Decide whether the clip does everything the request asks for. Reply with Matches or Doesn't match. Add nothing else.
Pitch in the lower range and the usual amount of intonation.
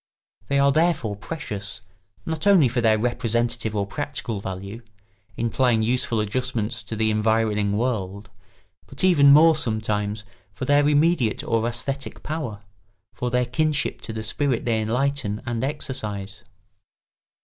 Matches